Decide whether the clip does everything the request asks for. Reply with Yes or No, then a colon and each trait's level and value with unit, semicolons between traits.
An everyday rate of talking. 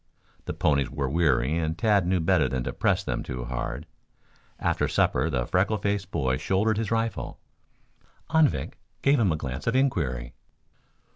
Yes: average, 160 wpm